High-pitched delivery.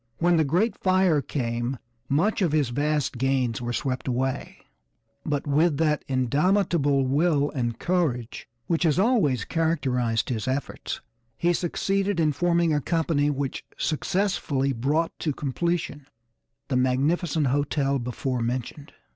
No: medium, 145 Hz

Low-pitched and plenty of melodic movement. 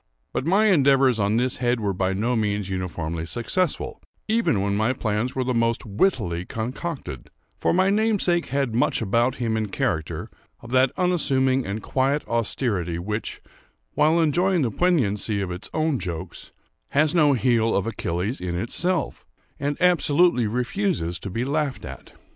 Yes: low, 125 Hz; wide, 6.5 semitones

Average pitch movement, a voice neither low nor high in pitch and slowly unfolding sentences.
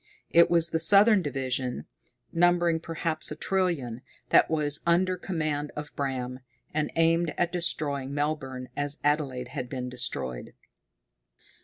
Yes: average, 4.1 semitones; medium, 150 Hz; slow, 130 wpm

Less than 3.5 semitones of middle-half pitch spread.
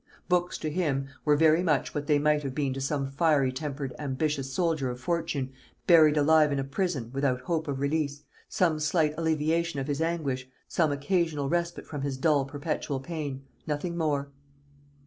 Yes: average, 2.8 semitones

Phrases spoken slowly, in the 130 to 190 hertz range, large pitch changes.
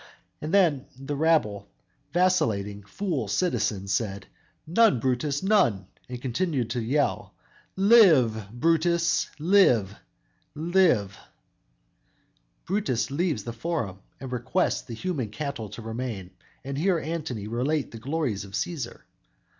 Yes: slow, 115 wpm; low, 135 Hz; wide, 7.0 semitones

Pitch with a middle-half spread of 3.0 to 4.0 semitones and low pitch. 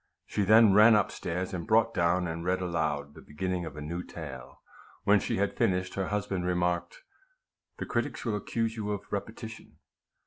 Yes: average, 3.5 semitones; very low, 95 Hz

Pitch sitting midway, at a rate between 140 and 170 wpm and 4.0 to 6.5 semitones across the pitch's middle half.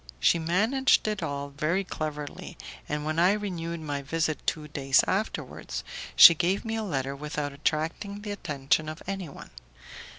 Yes: medium, 160 Hz; average, 155 wpm; average, 4.9 semitones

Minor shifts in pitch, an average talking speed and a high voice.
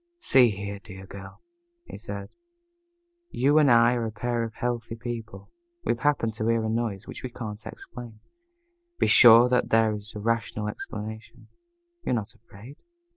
No: narrow, 2.1 semitones; average, 165 wpm; low, 115 Hz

